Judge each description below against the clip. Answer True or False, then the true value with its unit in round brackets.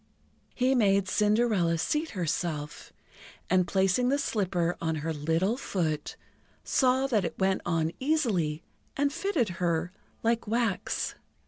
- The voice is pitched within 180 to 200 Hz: True (190 Hz)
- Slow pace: True (125 wpm)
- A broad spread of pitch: True (6.4 semitones)